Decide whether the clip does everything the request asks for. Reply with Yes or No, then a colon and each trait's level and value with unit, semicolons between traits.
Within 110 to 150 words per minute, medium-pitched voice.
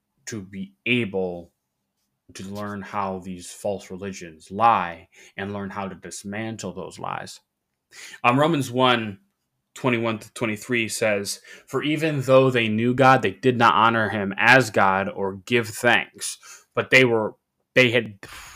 No: average, 140 wpm; low, 105 Hz